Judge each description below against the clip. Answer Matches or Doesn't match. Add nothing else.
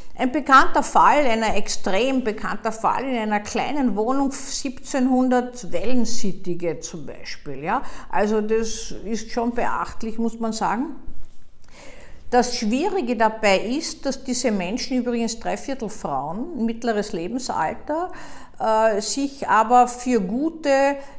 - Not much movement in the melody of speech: Doesn't match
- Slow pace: Matches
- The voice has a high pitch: Matches